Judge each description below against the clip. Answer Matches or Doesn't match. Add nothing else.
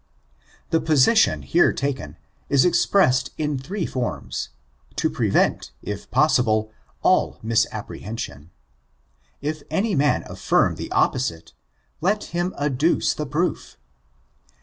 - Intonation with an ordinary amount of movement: Doesn't match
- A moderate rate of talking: Doesn't match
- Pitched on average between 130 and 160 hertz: Matches